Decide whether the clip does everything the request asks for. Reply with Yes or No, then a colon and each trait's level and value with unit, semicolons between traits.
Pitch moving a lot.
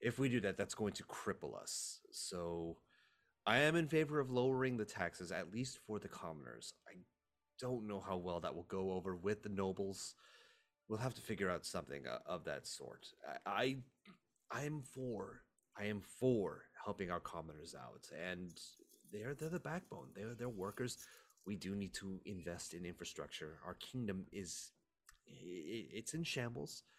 Yes: wide, 5.8 semitones